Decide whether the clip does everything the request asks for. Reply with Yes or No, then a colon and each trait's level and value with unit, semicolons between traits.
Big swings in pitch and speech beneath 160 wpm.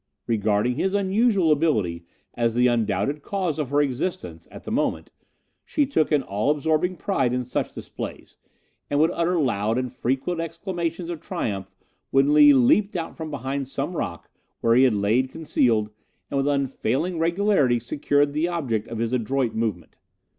No: wide, 5.8 semitones; average, 165 wpm